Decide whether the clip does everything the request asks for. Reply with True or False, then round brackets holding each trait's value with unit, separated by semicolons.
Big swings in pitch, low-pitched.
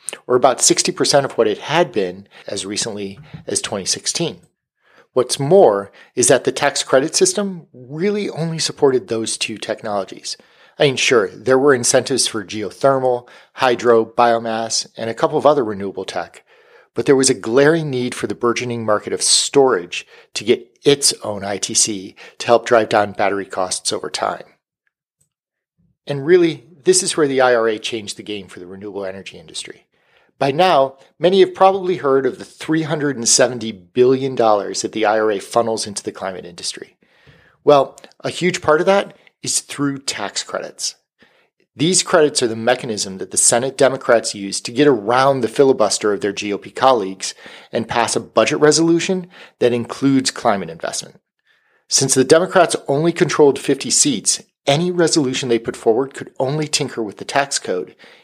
True (5.7 semitones; 130 Hz)